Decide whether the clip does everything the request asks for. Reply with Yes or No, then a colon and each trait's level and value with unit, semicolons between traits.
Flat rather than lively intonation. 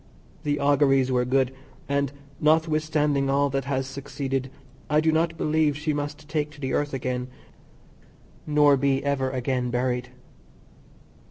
Yes: narrow, 2.0 semitones